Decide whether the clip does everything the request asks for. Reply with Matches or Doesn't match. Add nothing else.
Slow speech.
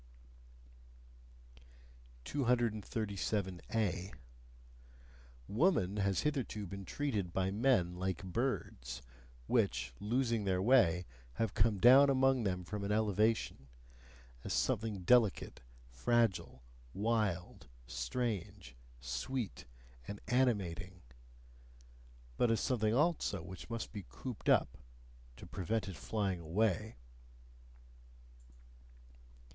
Matches